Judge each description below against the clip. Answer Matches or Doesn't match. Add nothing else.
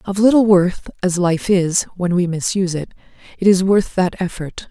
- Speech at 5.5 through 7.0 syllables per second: Doesn't match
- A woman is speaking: Matches